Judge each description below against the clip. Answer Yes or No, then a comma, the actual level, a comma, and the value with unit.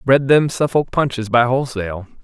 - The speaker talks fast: No, average, 160 wpm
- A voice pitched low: Yes, low, 125 Hz